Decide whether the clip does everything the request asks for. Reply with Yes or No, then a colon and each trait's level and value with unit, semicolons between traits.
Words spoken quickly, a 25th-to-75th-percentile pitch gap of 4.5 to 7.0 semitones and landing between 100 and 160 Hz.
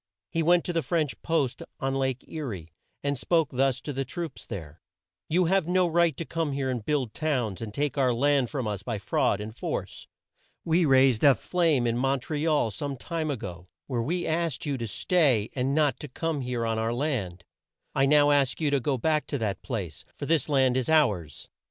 Yes: fast, 215 wpm; average, 4.8 semitones; low, 135 Hz